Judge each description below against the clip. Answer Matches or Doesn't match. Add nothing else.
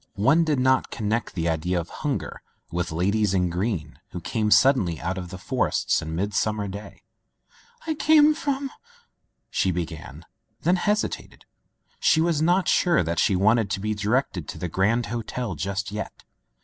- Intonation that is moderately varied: Doesn't match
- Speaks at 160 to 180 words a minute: Matches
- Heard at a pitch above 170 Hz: Doesn't match